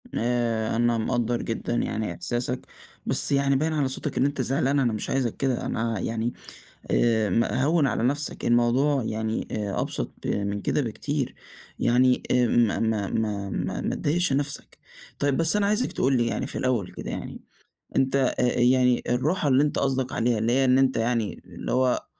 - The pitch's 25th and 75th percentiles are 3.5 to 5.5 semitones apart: No, average, 3.0 semitones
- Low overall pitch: Yes, low, 125 Hz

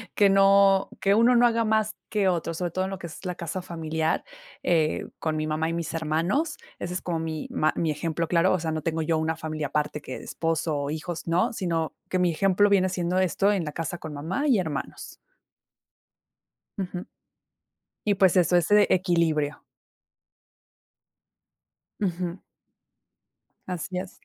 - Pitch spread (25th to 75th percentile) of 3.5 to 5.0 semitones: No, average, 3.1 semitones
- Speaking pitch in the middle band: Yes, medium, 175 Hz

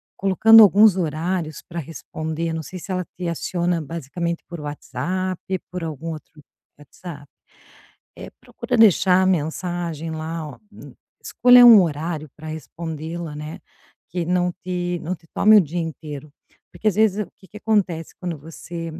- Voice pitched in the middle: Yes, medium, 170 Hz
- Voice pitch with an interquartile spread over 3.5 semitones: No, average, 2.7 semitones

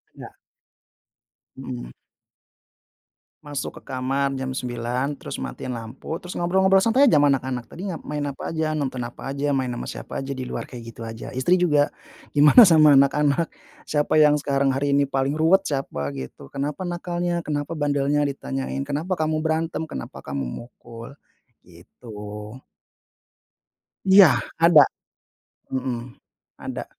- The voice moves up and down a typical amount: Yes, average, 3.7 semitones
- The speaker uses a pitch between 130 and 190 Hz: Yes, medium, 140 Hz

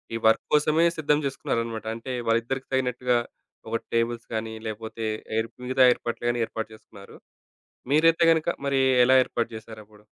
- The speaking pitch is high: No, low, 120 Hz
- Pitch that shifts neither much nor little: Yes, average, 3.1 semitones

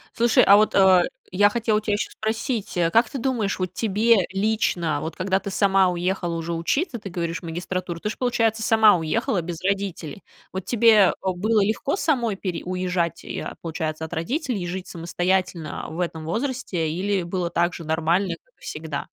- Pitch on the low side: No, high, 190 Hz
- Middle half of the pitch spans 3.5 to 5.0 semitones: Yes, average, 4.1 semitones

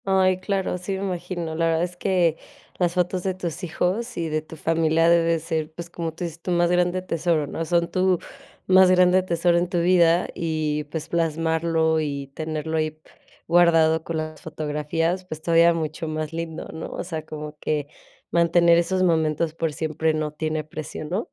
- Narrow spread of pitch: Yes, narrow, 2.0 semitones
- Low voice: No, medium, 165 Hz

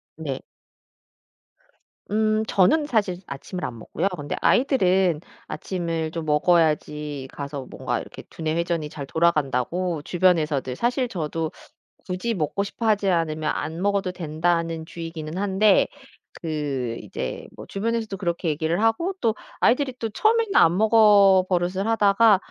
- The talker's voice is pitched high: No, medium, 175 Hz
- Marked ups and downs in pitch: No, average, 4.8 semitones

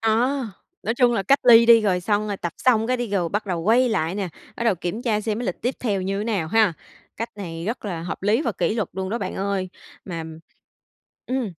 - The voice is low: No, high, 210 Hz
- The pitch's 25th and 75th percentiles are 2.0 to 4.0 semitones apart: Yes, average, 3.6 semitones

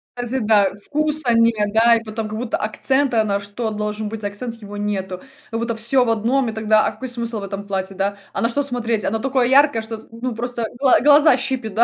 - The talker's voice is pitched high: Yes, high, 225 Hz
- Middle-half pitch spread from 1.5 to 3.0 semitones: Yes, average, 2.7 semitones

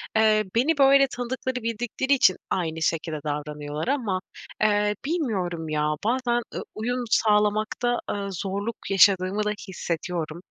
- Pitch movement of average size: No, wide, 5.7 semitones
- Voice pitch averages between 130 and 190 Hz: No, high, 210 Hz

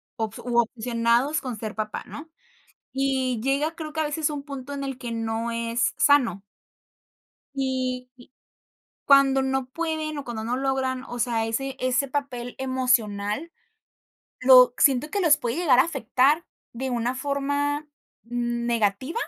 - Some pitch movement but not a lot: Yes, average, 3.0 semitones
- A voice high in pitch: Yes, very high, 260 Hz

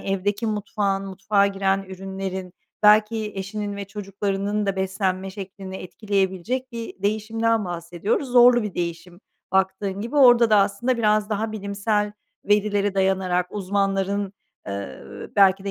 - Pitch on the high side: Yes, high, 200 Hz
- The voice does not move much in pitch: Yes, narrow, 1.7 semitones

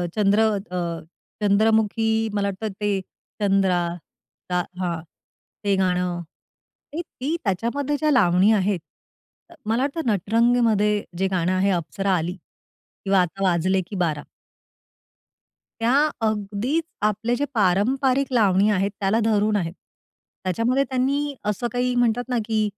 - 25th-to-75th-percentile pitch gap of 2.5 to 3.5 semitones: No, average, 4.1 semitones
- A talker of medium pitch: No, high, 210 Hz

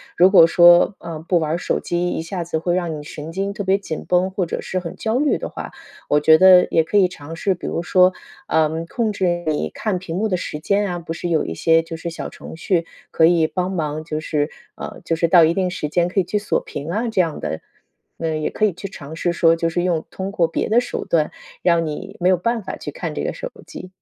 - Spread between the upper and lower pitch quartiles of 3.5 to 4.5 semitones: No, narrow, 2.6 semitones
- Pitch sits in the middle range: Yes, medium, 175 Hz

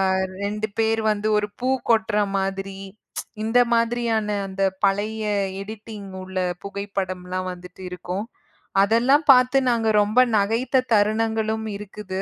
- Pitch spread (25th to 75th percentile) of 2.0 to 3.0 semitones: Yes, narrow, 2.4 semitones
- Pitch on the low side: No, high, 210 Hz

